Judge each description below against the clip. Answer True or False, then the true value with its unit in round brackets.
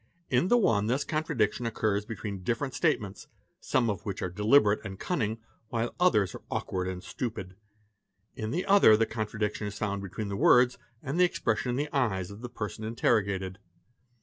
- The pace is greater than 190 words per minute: False (180 wpm)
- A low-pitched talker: True (110 Hz)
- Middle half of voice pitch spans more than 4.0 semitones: False (3.6 semitones)